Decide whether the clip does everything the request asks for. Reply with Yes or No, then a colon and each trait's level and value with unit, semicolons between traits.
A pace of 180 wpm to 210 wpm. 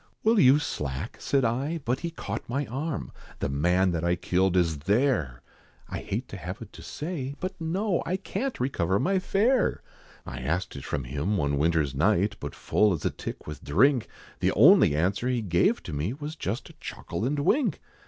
Yes: average, 195 wpm